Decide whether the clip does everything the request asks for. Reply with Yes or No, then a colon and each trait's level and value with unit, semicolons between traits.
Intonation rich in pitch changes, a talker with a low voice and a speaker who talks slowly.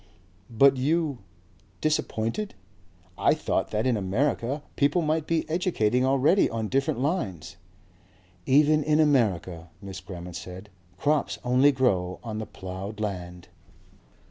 Yes: wide, 7.6 semitones; low, 120 Hz; slow, 125 wpm